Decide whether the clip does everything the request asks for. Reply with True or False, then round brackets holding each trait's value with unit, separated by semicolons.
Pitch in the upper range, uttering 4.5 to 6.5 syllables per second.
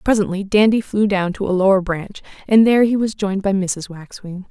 True (200 Hz; 5.5 syllables/s)